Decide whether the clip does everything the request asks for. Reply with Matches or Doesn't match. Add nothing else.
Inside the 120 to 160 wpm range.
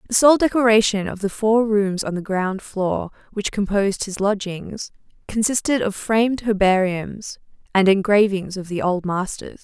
Matches